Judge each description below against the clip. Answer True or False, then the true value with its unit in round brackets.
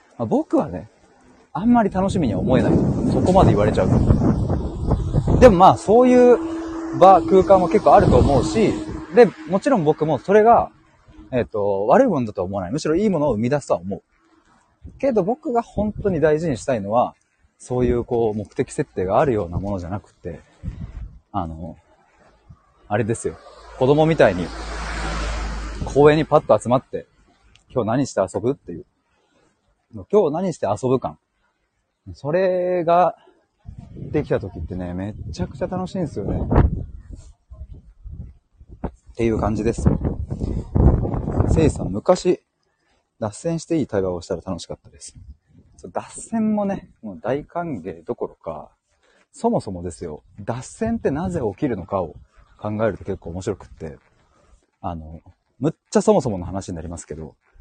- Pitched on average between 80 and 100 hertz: False (130 Hz)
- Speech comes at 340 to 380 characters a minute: False (295 characters per minute)